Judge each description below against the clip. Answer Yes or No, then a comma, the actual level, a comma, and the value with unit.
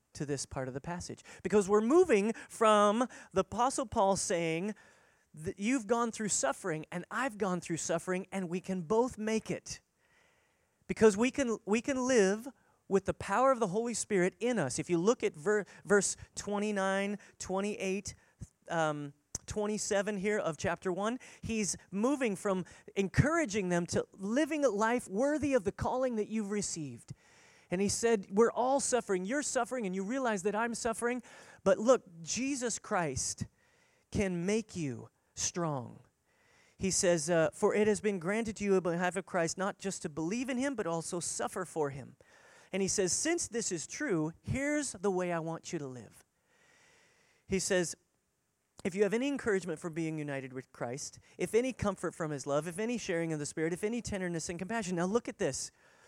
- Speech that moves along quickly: No, average, 180 wpm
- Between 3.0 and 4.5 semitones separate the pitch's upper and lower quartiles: No, average, 5.0 semitones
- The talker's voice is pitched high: Yes, high, 200 Hz